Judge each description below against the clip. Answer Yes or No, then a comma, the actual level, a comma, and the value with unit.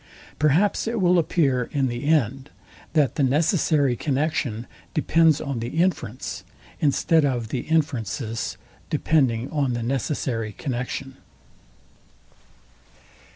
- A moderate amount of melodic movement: Yes, average, 4.3 semitones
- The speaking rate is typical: No, slow, 110 wpm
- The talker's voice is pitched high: No, medium, 140 Hz